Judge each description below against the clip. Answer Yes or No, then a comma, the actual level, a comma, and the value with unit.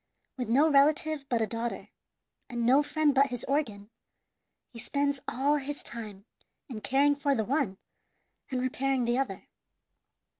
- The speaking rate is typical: Yes, average, 150 wpm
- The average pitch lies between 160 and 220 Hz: No, very high, 270 Hz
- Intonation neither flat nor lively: Yes, average, 3.3 semitones